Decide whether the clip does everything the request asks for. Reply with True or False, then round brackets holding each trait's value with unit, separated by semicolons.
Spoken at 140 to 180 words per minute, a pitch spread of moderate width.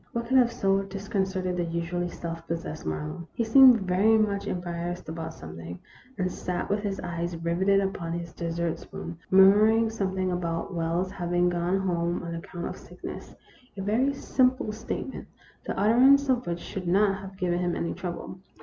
True (175 wpm; 3.0 semitones)